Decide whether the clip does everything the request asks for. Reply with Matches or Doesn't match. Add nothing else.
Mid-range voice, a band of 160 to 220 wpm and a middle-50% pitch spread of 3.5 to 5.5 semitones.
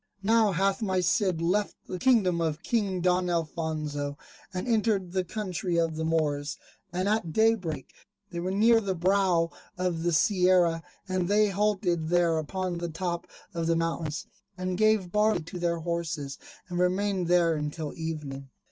Doesn't match